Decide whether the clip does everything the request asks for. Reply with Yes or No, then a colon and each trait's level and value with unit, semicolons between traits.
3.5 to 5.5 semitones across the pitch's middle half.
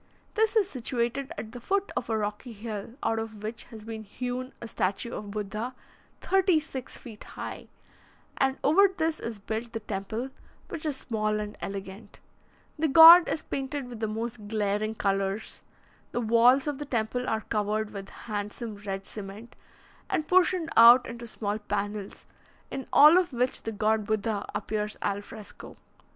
Yes: average, 3.9 semitones